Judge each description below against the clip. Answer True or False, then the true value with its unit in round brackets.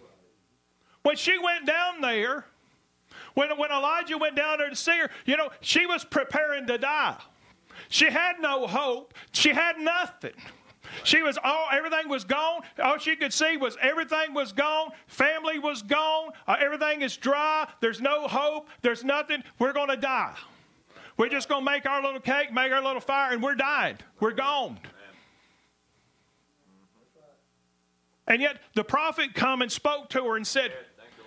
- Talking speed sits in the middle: True (160 wpm)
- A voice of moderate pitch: False (280 Hz)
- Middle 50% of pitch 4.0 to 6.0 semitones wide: False (3.3 semitones)